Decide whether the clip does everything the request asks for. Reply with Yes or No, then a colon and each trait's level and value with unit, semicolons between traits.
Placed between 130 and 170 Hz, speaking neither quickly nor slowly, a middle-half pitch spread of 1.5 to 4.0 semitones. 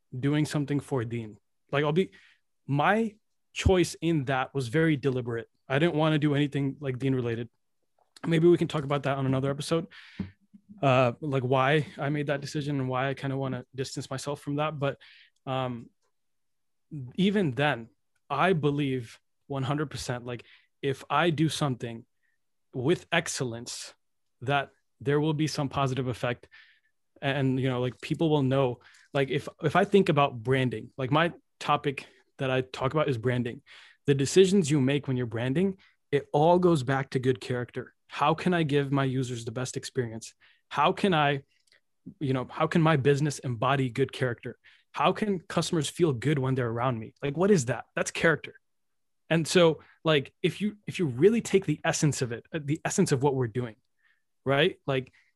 Yes: medium, 140 Hz; average, 180 wpm; average, 3.3 semitones